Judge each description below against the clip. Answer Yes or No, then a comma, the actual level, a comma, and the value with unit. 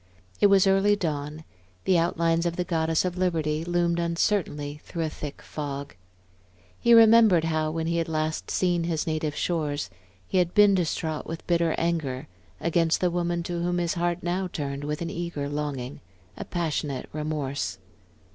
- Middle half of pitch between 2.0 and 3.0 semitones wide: Yes, narrow, 2.4 semitones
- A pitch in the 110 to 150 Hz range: No, medium, 165 Hz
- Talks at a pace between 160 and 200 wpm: Yes, average, 165 wpm